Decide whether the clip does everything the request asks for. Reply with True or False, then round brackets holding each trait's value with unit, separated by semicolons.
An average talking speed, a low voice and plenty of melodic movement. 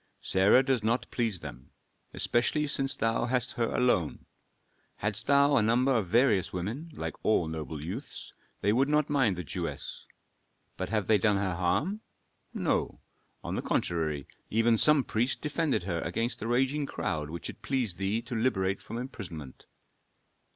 True (160 wpm; 115 Hz; 5.8 semitones)